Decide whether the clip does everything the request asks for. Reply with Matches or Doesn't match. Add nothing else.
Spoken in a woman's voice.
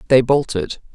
Matches